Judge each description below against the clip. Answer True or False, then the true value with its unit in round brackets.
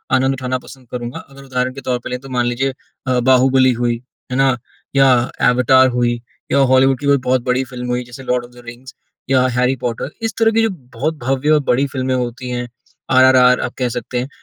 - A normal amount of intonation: False (1.3 semitones)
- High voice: False (130 Hz)